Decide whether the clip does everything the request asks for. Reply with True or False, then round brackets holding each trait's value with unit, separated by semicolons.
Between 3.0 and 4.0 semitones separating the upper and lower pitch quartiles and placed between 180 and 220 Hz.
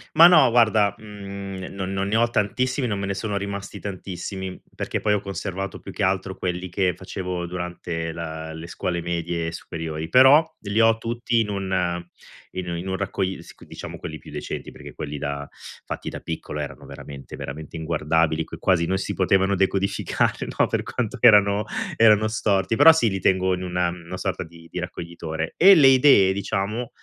False (3.3 semitones; 95 Hz)